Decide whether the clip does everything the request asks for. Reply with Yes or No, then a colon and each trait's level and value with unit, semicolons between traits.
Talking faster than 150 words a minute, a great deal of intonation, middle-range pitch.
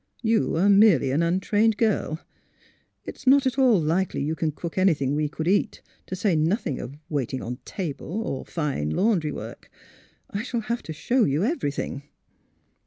Yes: average, 175 wpm; wide, 6.5 semitones; medium, 175 Hz